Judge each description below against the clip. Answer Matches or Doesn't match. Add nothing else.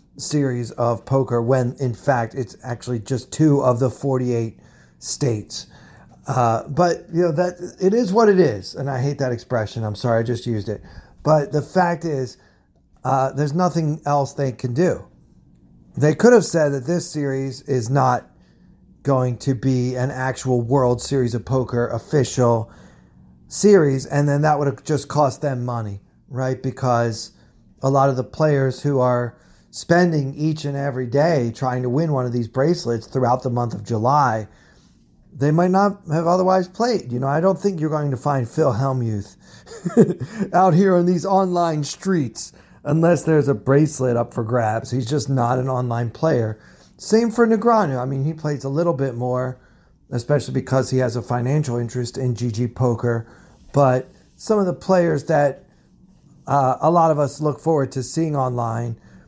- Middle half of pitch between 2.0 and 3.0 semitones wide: Doesn't match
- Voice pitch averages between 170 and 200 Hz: Doesn't match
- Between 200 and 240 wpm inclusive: Doesn't match